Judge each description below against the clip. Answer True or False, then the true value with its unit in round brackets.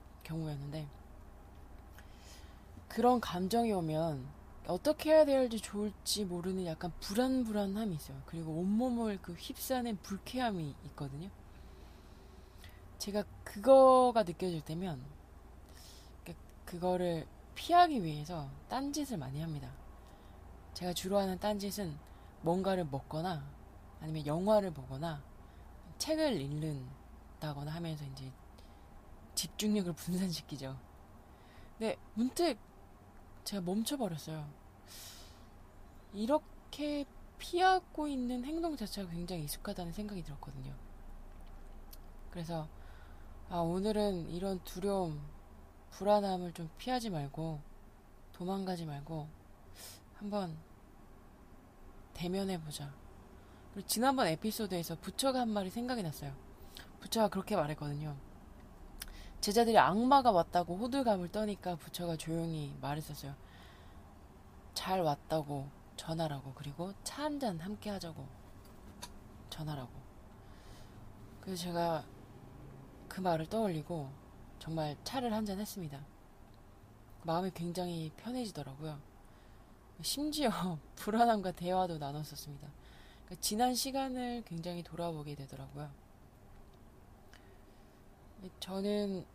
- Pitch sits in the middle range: True (160 Hz)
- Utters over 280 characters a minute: False (240 characters per minute)